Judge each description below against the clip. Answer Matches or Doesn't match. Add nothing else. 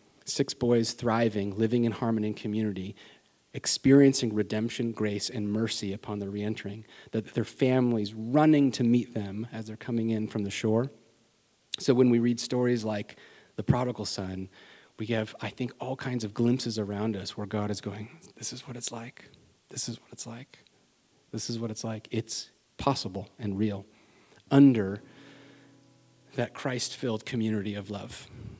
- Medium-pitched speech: Doesn't match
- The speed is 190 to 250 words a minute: Doesn't match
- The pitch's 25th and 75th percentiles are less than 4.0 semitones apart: Matches